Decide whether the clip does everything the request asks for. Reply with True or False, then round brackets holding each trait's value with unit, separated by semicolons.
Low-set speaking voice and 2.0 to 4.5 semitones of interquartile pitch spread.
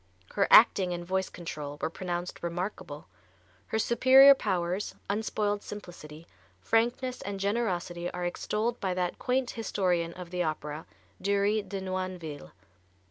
False (185 Hz; 3.4 semitones)